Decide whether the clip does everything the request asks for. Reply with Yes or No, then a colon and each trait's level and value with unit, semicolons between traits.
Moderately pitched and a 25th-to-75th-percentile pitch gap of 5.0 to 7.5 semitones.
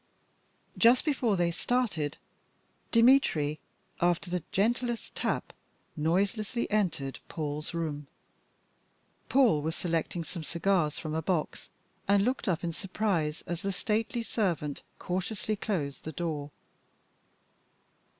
Yes: medium, 175 Hz; wide, 5.5 semitones